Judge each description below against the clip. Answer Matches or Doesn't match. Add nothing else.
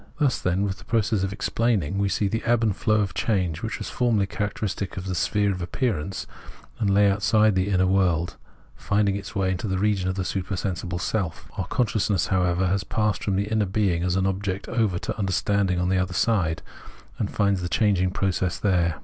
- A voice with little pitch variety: Matches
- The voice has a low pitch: Matches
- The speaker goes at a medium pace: Doesn't match